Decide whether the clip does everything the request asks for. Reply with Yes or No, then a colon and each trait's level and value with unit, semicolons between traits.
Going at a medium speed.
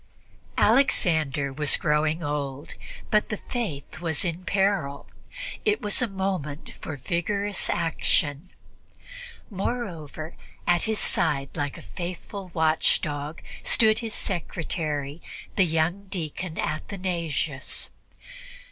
No: slow, 105 wpm